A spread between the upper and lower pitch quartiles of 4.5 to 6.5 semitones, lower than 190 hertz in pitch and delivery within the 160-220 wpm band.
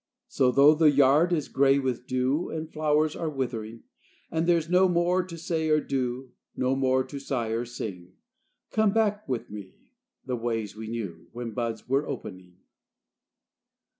Yes: average, 5.2 semitones; low, 135 Hz; average, 165 wpm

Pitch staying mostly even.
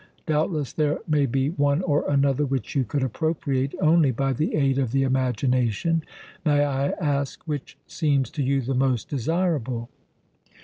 Yes: narrow, 2.3 semitones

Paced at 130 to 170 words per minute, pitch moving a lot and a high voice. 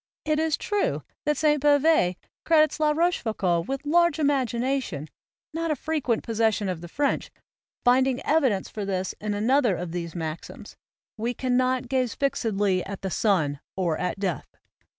Yes: average, 150 wpm; wide, 7.2 semitones; high, 245 Hz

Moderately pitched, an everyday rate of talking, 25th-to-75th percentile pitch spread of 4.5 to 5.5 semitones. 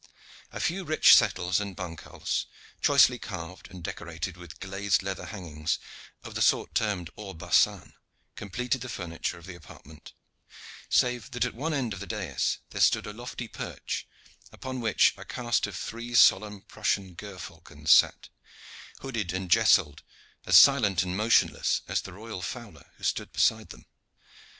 No: low, 100 Hz; average, 155 wpm; average, 4.9 semitones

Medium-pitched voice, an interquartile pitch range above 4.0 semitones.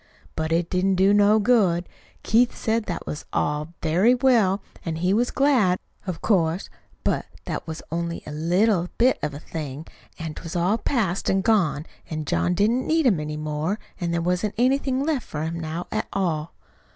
Yes: medium, 180 Hz; average, 5.2 semitones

